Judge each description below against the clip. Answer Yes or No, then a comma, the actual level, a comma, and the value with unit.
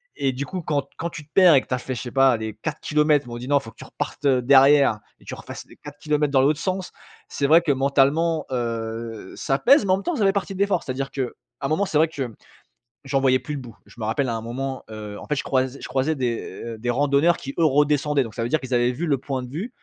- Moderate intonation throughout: Yes, average, 3.4 semitones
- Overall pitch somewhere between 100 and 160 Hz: Yes, medium, 140 Hz